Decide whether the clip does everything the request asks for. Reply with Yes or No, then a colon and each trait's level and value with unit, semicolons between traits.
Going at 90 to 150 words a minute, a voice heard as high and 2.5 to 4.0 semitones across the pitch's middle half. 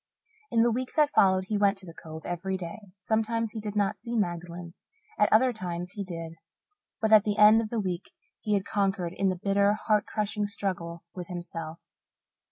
No: average, 195 wpm; high, 200 Hz; average, 3.4 semitones